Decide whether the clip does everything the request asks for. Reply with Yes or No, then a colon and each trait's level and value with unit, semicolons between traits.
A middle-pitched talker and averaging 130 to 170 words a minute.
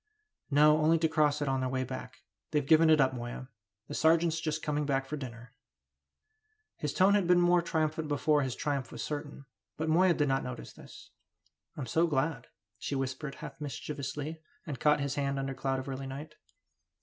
No: medium, 145 Hz; average, 190 wpm